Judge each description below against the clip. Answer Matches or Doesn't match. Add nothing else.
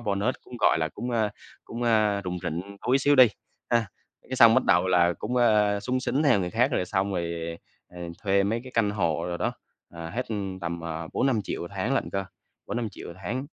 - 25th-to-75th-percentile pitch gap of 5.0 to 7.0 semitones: Matches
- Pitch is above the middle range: Doesn't match